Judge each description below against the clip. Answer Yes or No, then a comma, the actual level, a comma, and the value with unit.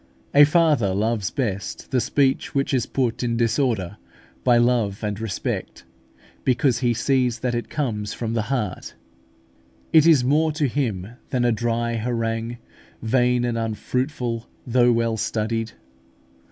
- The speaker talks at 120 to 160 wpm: Yes, average, 140 wpm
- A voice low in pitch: Yes, low, 120 Hz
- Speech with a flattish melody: Yes, narrow, 2.3 semitones